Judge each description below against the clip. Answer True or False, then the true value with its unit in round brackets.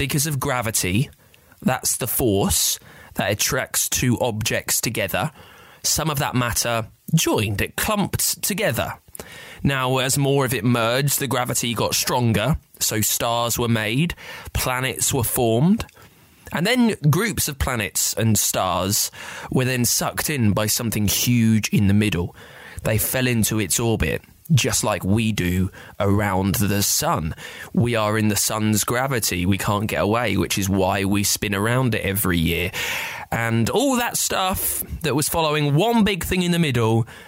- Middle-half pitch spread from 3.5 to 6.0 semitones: True (4.1 semitones)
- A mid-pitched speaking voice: False (115 Hz)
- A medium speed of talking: True (155 wpm)